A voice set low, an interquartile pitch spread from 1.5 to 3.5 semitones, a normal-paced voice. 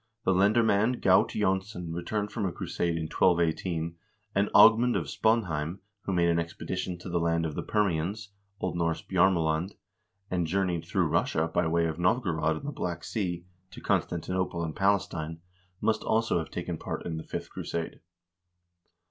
Yes: very low, 90 Hz; average, 3.2 semitones; average, 165 wpm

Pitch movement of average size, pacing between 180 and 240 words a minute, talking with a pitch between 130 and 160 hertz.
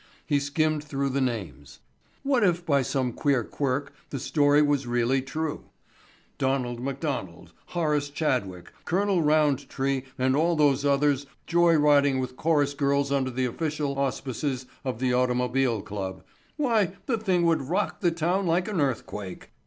No: average, 3.4 semitones; average, 145 wpm; medium, 140 Hz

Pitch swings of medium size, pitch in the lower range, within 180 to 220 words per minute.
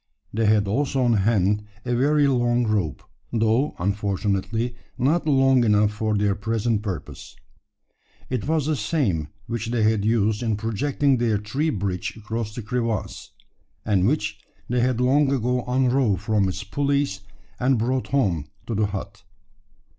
No: average, 3.6 semitones; low, 115 Hz; average, 150 wpm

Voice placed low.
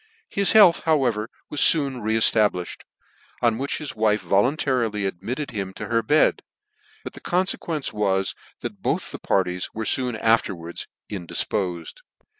Yes: low, 110 Hz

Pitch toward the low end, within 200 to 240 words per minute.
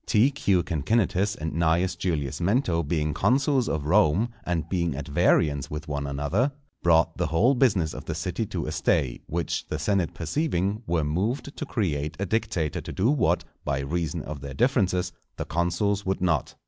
No: very low, 85 Hz; average, 180 wpm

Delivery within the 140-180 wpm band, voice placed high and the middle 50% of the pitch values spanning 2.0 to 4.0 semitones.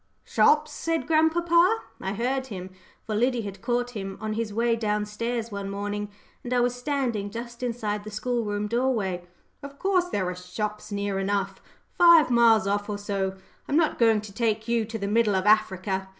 No: average, 190 wpm; high, 215 Hz; average, 3.2 semitones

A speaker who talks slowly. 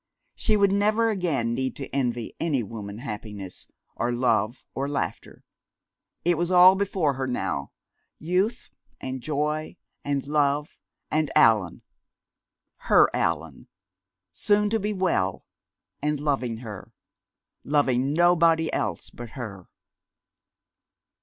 Yes: slow, 115 wpm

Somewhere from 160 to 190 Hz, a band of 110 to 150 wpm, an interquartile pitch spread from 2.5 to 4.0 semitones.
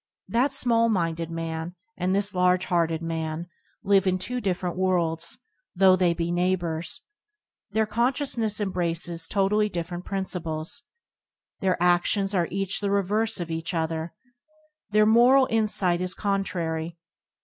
Yes: medium, 185 Hz; average, 140 wpm; average, 3.3 semitones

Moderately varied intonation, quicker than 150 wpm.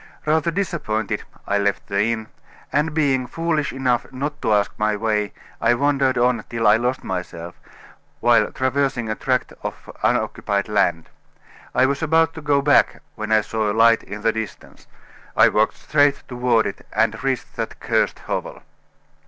Yes: average, 4.7 semitones; average, 165 wpm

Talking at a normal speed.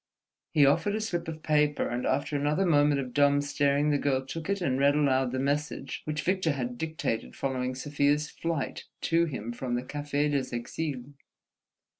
Yes: average, 180 wpm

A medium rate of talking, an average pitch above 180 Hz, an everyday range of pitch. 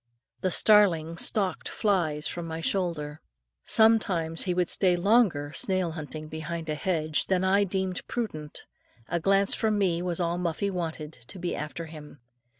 No: average, 155 wpm; medium, 175 Hz; average, 3.4 semitones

